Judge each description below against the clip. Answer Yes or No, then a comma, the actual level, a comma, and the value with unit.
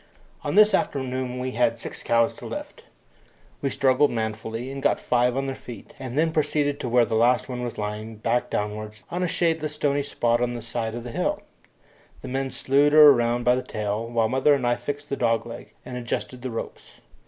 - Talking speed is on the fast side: Yes, fast, 210 wpm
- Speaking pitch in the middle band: No, low, 125 Hz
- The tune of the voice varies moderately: Yes, average, 3.1 semitones